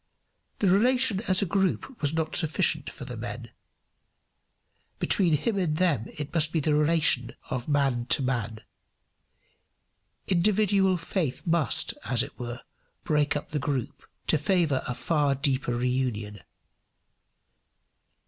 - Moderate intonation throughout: No, wide, 5.7 semitones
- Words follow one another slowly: Yes, slow, 130 wpm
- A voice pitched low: No, medium, 150 Hz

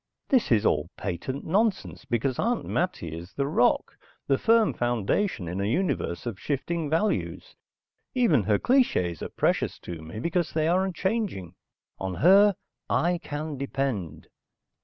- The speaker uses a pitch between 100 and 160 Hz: Yes, medium, 140 Hz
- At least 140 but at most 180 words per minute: Yes, average, 145 wpm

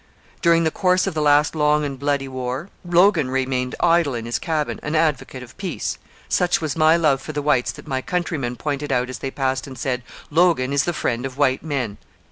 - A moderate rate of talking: No, fast, 210 wpm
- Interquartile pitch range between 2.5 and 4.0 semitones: Yes, average, 3.7 semitones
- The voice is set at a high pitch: No, medium, 145 Hz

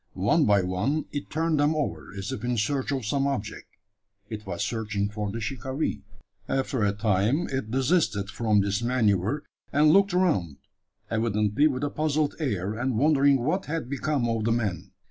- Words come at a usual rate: Yes, average, 175 wpm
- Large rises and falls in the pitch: Yes, wide, 5.8 semitones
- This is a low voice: Yes, low, 120 Hz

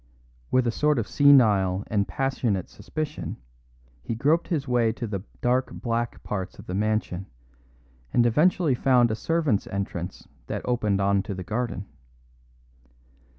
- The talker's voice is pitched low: Yes, low, 115 Hz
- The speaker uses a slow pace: No, average, 145 wpm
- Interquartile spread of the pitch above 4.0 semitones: Yes, average, 5.1 semitones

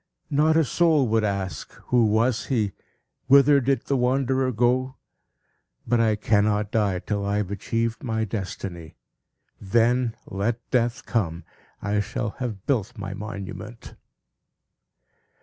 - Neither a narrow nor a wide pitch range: Yes, average, 3.6 semitones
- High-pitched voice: No, low, 115 Hz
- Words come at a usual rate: No, slow, 130 wpm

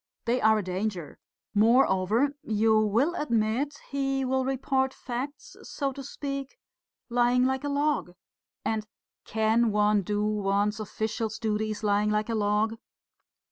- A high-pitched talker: Yes, high, 220 Hz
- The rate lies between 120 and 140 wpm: Yes, slow, 135 wpm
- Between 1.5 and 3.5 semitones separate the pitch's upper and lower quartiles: No, average, 4.0 semitones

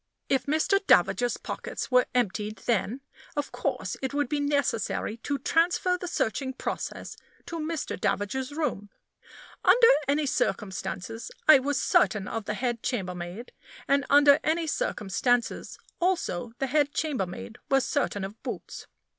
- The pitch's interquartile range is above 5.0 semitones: Yes, wide, 5.4 semitones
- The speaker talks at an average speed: Yes, average, 145 wpm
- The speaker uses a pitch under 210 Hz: No, very high, 260 Hz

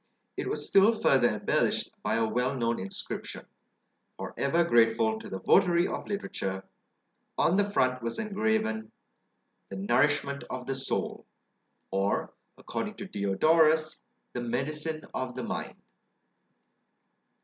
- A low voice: Yes, low, 130 Hz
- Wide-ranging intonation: Yes, wide, 6.2 semitones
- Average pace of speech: No, slow, 125 wpm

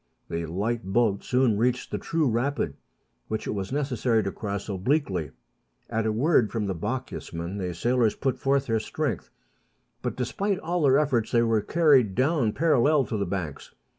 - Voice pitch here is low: Yes, low, 115 Hz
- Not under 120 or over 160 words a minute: No, average, 170 wpm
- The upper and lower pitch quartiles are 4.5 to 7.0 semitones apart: Yes, average, 5.3 semitones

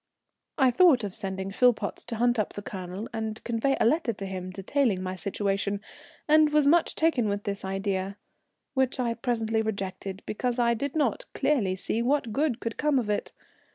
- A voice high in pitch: Yes, high, 225 Hz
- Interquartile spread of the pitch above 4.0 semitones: Yes, average, 4.9 semitones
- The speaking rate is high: No, average, 185 wpm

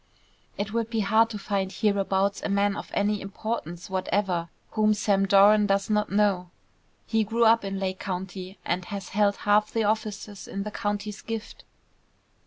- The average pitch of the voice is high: Yes, high, 205 Hz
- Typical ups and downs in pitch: No, narrow, 1.5 semitones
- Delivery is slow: No, average, 170 wpm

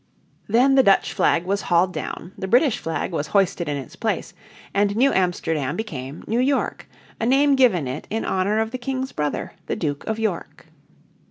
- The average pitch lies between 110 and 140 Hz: No, high, 200 Hz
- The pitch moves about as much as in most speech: No, wide, 6.6 semitones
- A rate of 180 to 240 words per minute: Yes, average, 185 wpm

